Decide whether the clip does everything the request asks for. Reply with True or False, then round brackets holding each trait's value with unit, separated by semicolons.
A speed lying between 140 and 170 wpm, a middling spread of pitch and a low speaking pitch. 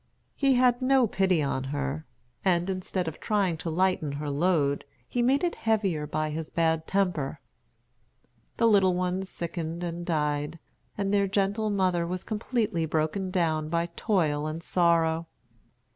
False (150 wpm; 3.9 semitones; 175 Hz)